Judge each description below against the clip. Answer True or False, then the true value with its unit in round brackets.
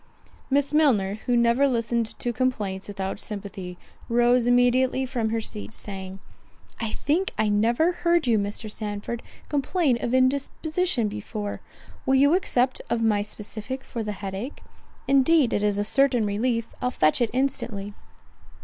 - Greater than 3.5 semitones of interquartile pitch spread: True (4.1 semitones)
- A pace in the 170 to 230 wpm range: False (150 wpm)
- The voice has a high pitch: True (235 Hz)